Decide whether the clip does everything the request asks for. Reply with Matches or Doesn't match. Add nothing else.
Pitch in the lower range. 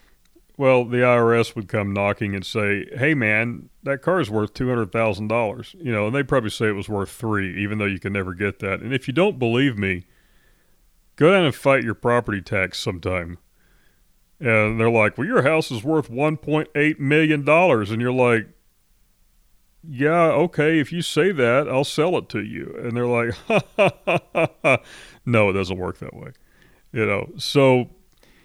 Matches